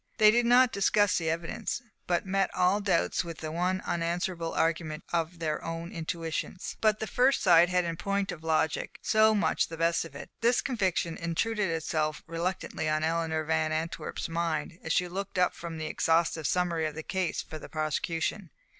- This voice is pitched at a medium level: Yes, medium, 170 Hz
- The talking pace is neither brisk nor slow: Yes, average, 185 wpm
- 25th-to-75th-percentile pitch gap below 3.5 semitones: Yes, narrow, 2.6 semitones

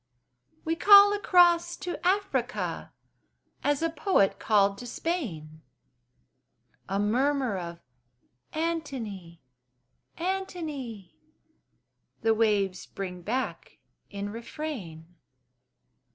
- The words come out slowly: Yes, slow, 80 wpm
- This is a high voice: Yes, high, 245 Hz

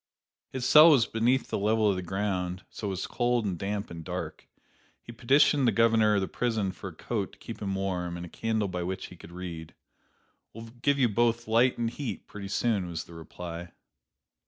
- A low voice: Yes, low, 105 Hz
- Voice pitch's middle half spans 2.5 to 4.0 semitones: No, average, 4.4 semitones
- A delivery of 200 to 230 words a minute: Yes, fast, 205 wpm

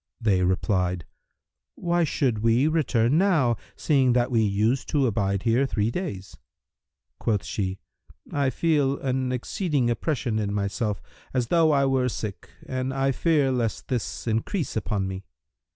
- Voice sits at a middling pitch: No, low, 120 Hz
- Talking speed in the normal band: Yes, average, 145 wpm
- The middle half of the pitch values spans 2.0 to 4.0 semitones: No, average, 4.7 semitones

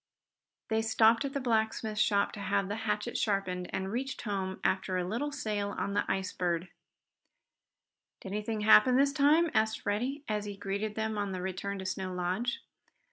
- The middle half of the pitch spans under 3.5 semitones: Yes, narrow, 2.6 semitones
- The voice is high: Yes, high, 210 Hz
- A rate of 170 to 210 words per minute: Yes, average, 180 wpm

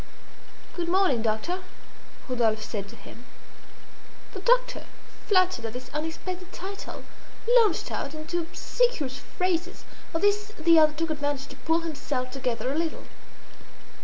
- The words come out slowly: Yes, slow, 130 wpm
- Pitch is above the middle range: Yes, very high, 320 Hz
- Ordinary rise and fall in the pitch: No, wide, 5.9 semitones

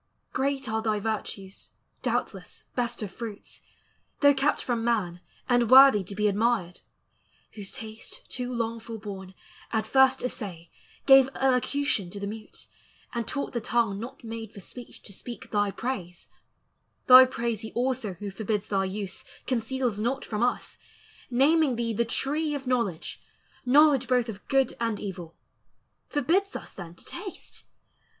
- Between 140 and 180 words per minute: Yes, average, 150 wpm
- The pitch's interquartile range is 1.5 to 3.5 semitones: No, average, 4.0 semitones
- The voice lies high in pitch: Yes, high, 230 Hz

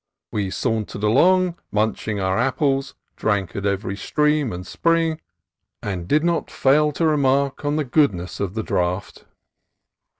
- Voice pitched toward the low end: Yes, low, 125 Hz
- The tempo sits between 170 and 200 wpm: No, average, 145 wpm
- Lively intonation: Yes, wide, 7.1 semitones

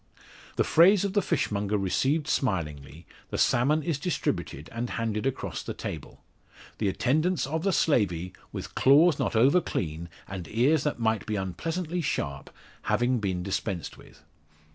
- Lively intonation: Yes, wide, 8.6 semitones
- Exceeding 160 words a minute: No, average, 150 wpm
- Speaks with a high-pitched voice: No, low, 120 Hz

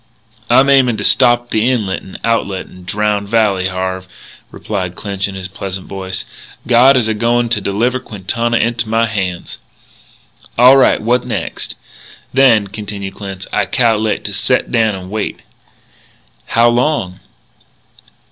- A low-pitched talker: Yes, low, 110 Hz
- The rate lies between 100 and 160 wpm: Yes, average, 145 wpm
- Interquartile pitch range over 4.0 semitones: No, average, 3.7 semitones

